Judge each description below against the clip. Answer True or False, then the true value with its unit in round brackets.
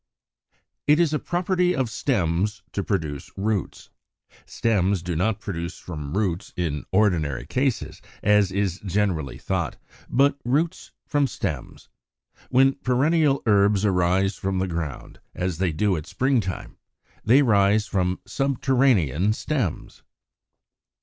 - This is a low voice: True (100 Hz)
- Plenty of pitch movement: True (6.5 semitones)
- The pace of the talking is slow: True (125 wpm)